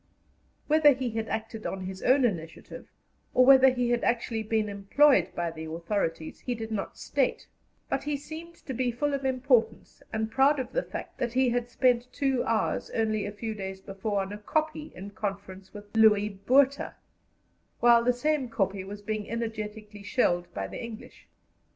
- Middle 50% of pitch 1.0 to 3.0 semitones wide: No, average, 4.2 semitones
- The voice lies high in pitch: Yes, high, 225 Hz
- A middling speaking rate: Yes, average, 180 wpm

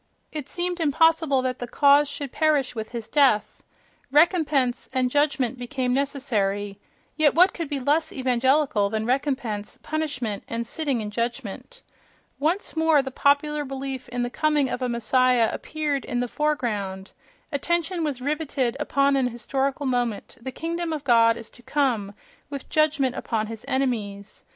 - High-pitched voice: Yes, very high, 265 Hz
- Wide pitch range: No, average, 3.8 semitones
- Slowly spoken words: No, average, 155 wpm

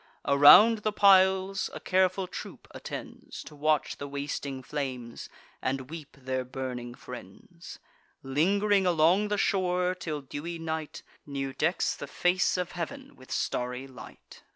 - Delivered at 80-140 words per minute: Yes, slow, 135 wpm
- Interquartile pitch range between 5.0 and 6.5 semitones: Yes, wide, 5.6 semitones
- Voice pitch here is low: No, medium, 155 Hz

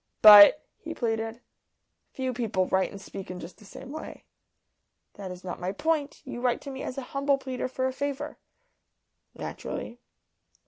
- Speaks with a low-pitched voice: No, high, 245 Hz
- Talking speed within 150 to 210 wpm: Yes, average, 170 wpm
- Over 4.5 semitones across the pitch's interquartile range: Yes, wide, 5.4 semitones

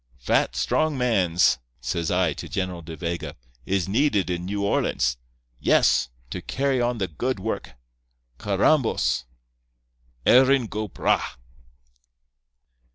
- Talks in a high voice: No, very low, 95 Hz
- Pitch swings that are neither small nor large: No, wide, 6.4 semitones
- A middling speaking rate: No, slow, 115 wpm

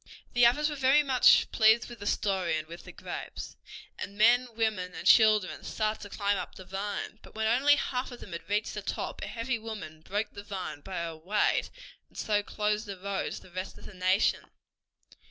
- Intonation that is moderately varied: Yes, average, 3.5 semitones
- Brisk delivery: Yes, fast, 210 wpm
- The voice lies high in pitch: Yes, high, 210 Hz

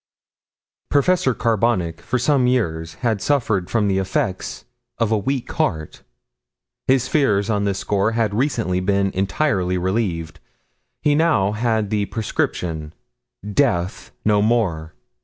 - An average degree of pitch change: Yes, average, 4.4 semitones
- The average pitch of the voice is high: No, low, 105 Hz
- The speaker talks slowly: Yes, slow, 125 wpm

